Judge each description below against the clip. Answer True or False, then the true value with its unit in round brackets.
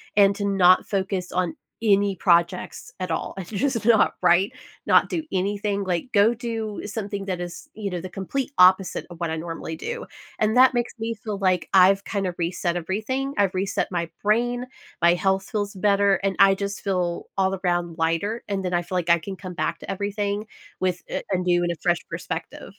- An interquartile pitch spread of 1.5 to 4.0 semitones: True (2.8 semitones)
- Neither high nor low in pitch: False (195 Hz)